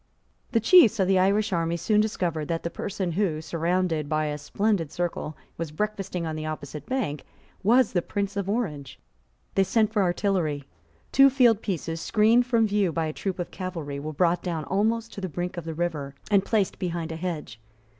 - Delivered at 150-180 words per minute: No, average, 195 wpm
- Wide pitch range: No, average, 4.5 semitones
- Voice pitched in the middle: Yes, medium, 180 Hz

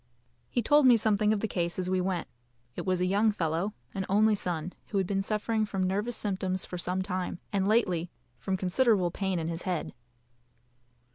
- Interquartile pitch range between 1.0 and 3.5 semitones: Yes, average, 2.7 semitones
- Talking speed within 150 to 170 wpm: No, average, 195 wpm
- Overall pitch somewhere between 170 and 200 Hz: Yes, high, 190 Hz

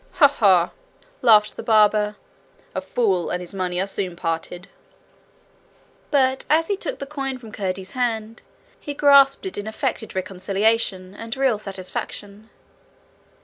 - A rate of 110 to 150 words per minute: Yes, average, 140 wpm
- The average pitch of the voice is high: Yes, high, 215 Hz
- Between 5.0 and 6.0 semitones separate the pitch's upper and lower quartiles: Yes, wide, 5.5 semitones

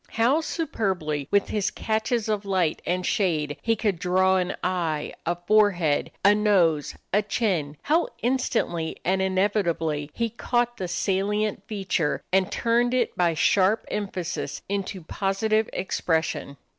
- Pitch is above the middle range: Yes, high, 195 Hz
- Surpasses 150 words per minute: No, slow, 135 wpm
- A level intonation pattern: No, average, 3.8 semitones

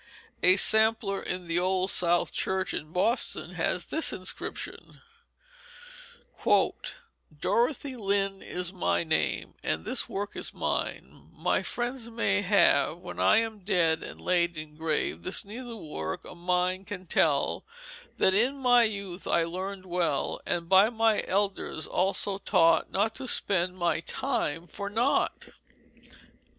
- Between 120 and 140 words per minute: Yes, slow, 135 wpm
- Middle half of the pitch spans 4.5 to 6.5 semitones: No, average, 3.8 semitones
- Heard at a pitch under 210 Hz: Yes, high, 190 Hz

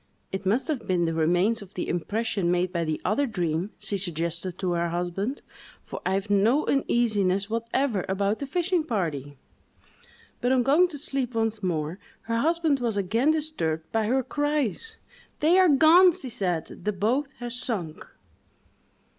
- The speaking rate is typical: Yes, average, 165 wpm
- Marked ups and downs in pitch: Yes, wide, 7.2 semitones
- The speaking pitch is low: No, high, 215 Hz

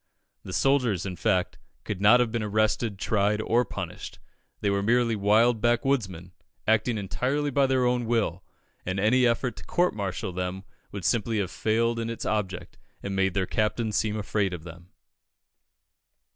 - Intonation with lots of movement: No, average, 3.5 semitones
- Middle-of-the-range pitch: No, low, 110 Hz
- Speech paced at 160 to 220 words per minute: Yes, average, 165 wpm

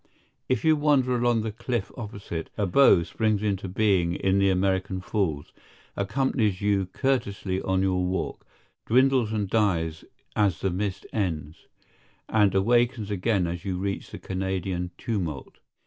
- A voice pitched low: Yes, low, 100 Hz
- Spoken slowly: No, average, 145 wpm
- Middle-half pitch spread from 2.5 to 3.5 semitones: Yes, average, 3.2 semitones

